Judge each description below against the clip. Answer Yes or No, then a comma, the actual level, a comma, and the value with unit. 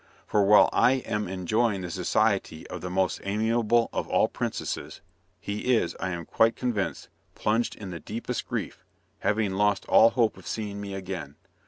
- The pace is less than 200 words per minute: Yes, average, 170 wpm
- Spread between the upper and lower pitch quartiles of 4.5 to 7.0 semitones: No, average, 3.1 semitones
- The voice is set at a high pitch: No, low, 105 Hz